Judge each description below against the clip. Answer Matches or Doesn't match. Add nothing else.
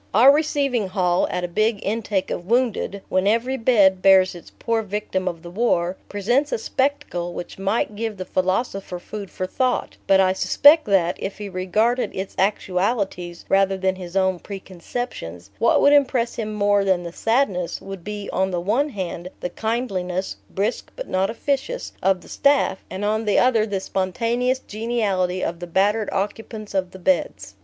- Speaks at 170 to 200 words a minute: Matches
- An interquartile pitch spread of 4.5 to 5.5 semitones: Doesn't match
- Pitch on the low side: Doesn't match